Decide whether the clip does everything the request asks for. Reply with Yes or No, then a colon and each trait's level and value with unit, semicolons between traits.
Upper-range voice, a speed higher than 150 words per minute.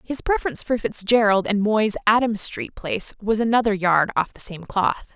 Yes: high, 215 Hz; average, 185 wpm